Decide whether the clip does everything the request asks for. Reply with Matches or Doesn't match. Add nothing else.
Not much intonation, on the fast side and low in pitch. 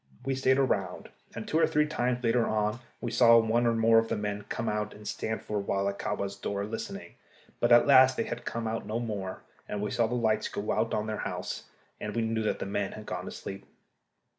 Matches